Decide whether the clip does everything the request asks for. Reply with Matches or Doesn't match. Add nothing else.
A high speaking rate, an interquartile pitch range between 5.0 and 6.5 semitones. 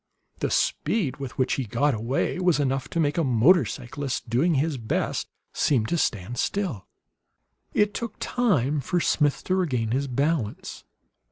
Doesn't match